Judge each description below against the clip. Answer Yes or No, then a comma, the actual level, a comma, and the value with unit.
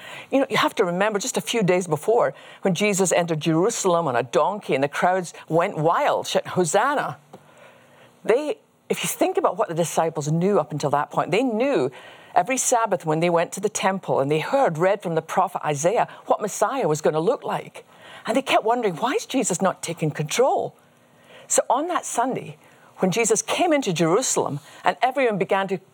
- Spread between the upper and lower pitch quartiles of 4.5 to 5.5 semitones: Yes, average, 5.2 semitones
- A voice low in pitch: No, high, 190 Hz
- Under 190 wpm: No, average, 200 wpm